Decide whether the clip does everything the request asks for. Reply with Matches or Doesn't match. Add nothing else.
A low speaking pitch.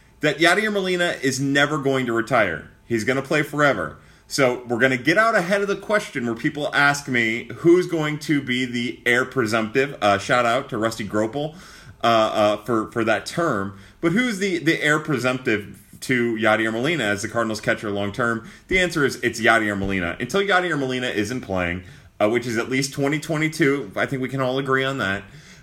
Matches